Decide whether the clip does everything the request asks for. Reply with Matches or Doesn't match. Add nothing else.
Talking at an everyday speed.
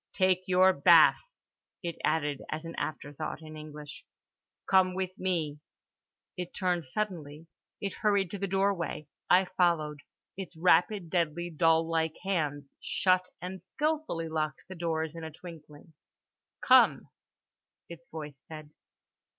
Doesn't match